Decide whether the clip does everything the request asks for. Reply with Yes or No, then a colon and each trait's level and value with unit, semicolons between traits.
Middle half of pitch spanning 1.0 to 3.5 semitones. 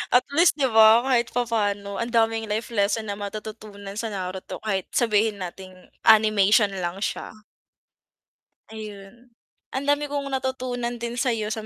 Yes: average, 3.0 semitones